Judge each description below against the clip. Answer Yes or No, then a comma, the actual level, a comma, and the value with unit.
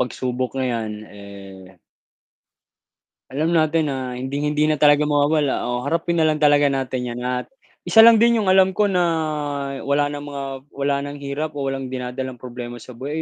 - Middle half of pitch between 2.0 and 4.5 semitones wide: Yes, average, 3.4 semitones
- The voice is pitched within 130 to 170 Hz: Yes, medium, 140 Hz